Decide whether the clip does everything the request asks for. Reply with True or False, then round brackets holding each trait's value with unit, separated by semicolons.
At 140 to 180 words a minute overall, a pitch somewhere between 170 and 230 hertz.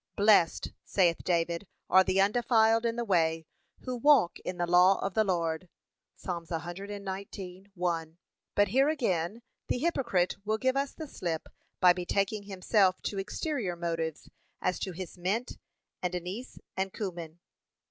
True (145 wpm; 190 Hz)